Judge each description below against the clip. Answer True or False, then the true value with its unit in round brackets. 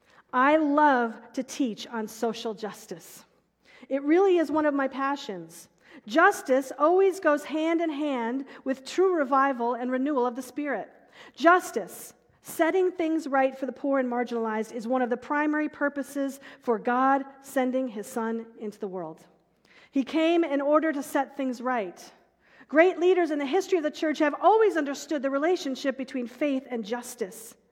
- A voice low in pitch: False (275 Hz)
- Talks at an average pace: True (165 wpm)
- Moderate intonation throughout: True (3.9 semitones)